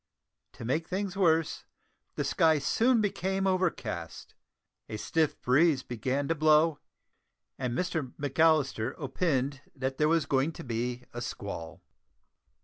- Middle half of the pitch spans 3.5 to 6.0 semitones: Yes, average, 4.7 semitones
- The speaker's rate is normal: No, slow, 130 wpm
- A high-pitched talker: No, medium, 150 Hz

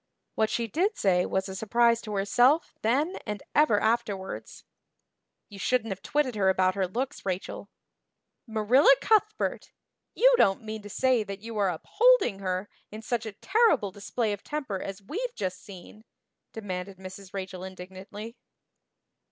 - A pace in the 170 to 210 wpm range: No, average, 150 wpm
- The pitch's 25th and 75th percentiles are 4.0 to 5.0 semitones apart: Yes, average, 4.4 semitones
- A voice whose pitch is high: Yes, high, 210 Hz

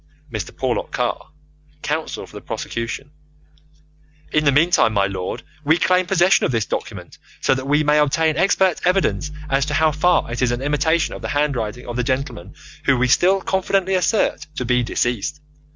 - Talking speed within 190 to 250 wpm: No, average, 180 wpm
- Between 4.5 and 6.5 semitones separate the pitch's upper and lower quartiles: Yes, average, 5.3 semitones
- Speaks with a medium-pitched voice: Yes, medium, 145 Hz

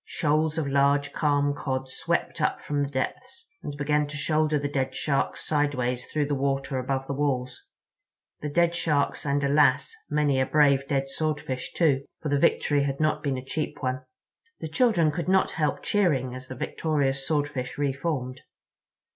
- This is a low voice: No, medium, 145 Hz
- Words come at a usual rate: Yes, average, 170 wpm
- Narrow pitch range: Yes, narrow, 2.0 semitones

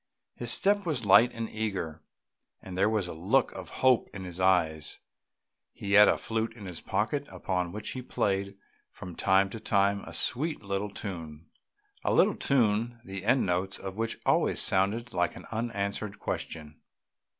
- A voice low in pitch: Yes, low, 100 Hz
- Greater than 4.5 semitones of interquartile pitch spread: No, average, 3.4 semitones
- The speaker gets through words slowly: No, average, 170 wpm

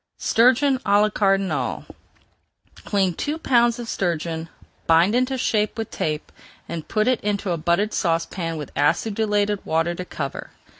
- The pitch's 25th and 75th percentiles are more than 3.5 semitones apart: Yes, average, 5.1 semitones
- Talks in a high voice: Yes, high, 200 Hz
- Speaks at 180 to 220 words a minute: No, average, 145 wpm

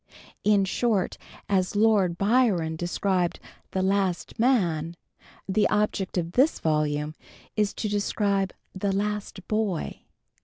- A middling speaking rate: No, slow, 115 wpm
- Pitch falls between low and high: No, high, 195 Hz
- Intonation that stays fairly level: No, average, 3.2 semitones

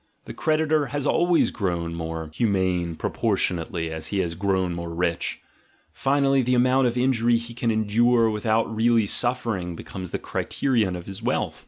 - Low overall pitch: Yes, low, 110 Hz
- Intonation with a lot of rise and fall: Yes, wide, 5.8 semitones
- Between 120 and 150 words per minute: No, average, 165 wpm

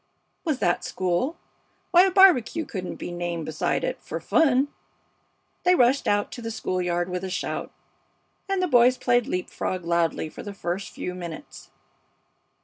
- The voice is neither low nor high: No, high, 205 Hz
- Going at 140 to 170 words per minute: Yes, average, 165 wpm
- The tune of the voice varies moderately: No, wide, 8.0 semitones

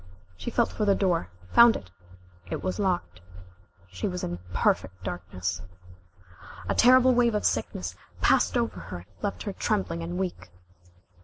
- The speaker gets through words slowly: No, average, 155 wpm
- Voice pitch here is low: No, medium, 175 Hz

